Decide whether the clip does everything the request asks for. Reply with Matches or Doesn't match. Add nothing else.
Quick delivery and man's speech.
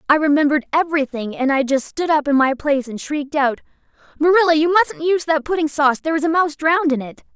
Doesn't match